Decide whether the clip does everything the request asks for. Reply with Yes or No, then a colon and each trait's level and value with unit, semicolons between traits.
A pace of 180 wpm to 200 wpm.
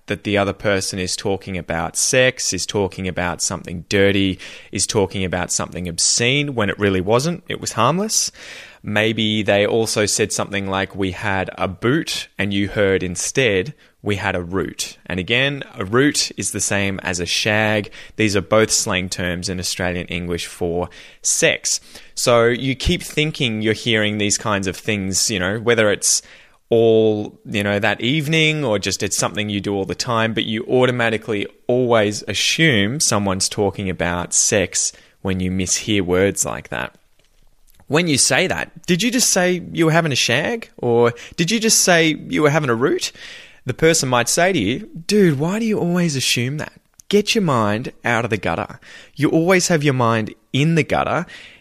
Yes: average, 185 wpm